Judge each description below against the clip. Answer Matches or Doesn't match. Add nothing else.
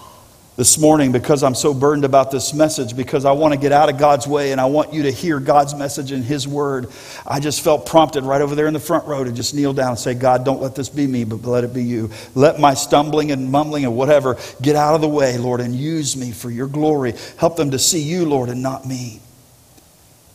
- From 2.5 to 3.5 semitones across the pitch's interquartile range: Matches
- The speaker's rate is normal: Doesn't match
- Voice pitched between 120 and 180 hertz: Matches